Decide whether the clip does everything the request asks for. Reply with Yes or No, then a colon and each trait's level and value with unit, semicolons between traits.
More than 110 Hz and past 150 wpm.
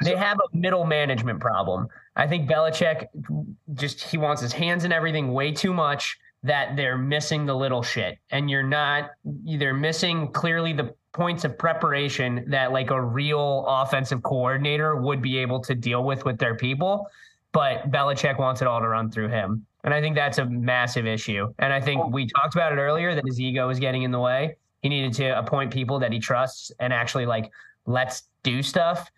Yes: low, 135 Hz; average, 195 wpm